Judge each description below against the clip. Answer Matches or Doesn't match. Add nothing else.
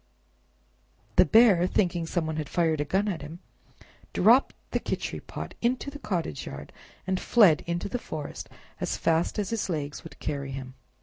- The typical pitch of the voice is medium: Matches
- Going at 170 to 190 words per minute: Matches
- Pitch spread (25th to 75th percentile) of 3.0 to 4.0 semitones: Doesn't match